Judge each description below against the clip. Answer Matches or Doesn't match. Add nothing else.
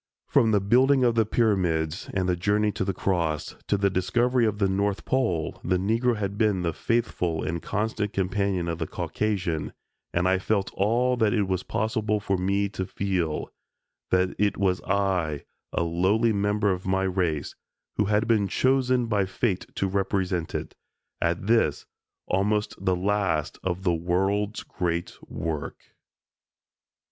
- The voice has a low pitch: Matches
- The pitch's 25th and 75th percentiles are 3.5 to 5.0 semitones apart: Doesn't match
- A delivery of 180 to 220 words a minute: Doesn't match